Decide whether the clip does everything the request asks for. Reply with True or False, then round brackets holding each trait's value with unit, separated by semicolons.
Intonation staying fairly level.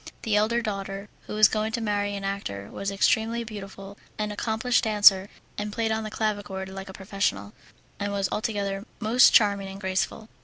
True (1.8 semitones)